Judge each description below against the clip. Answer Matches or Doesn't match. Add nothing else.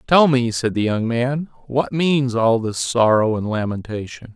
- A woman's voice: Doesn't match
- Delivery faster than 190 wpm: Doesn't match